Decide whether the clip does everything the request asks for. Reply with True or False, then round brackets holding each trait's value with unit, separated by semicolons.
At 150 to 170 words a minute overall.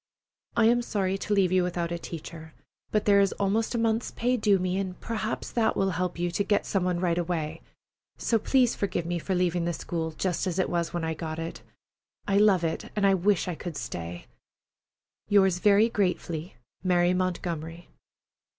False (190 wpm)